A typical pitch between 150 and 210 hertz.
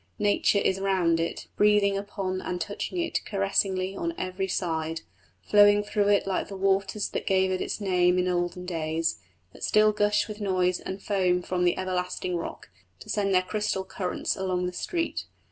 Yes: high, 190 Hz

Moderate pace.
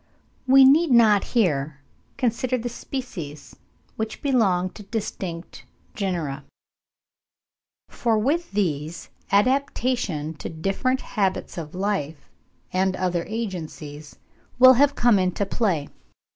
No: slow, 105 wpm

